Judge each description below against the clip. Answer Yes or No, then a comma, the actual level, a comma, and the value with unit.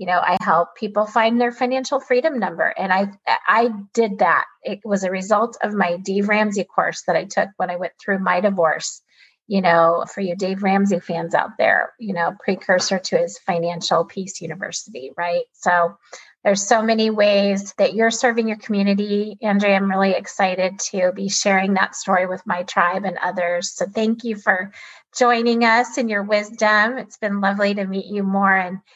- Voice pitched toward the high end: Yes, high, 200 Hz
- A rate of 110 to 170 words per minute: No, average, 190 wpm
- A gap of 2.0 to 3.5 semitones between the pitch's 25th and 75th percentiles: Yes, average, 3.0 semitones